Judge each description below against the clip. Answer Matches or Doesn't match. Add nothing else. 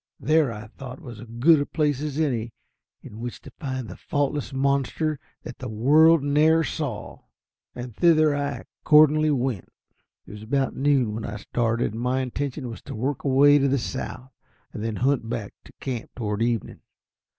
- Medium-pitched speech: Doesn't match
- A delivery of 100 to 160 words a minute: Doesn't match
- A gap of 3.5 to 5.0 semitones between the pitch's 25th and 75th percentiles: Matches